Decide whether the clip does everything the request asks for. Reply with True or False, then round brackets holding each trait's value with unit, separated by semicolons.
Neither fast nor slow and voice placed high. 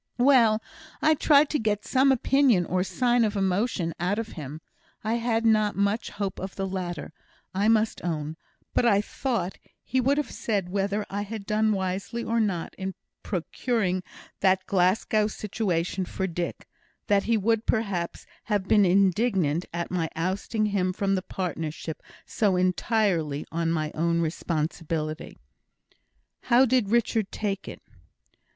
True (150 wpm; 200 Hz)